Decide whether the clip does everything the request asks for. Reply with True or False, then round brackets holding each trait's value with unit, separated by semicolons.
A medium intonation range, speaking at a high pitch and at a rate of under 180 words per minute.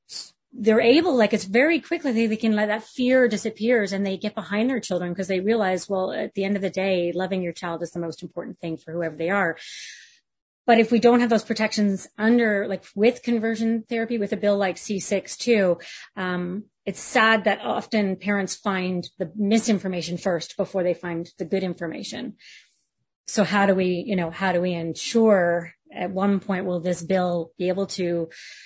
False (3.6 semitones; 195 Hz; 205 wpm)